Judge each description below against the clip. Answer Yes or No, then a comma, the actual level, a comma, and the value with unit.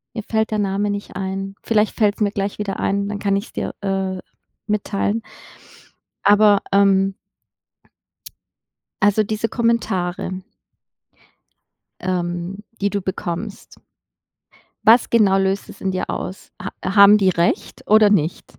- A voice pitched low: No, high, 200 Hz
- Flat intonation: Yes, narrow, 1.6 semitones